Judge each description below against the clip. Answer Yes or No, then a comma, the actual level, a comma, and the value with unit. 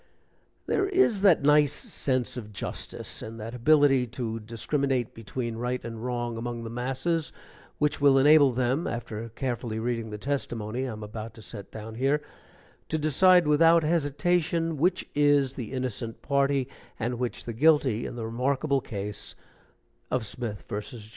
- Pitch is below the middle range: Yes, low, 125 Hz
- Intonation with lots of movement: No, average, 4.3 semitones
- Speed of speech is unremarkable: Yes, average, 155 wpm